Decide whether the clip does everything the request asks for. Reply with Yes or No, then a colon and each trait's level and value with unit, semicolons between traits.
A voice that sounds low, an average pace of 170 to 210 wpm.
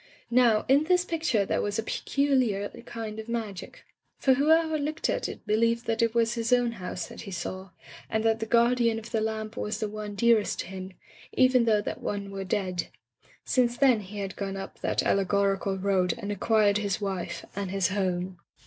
No: high, 215 Hz; average, 195 wpm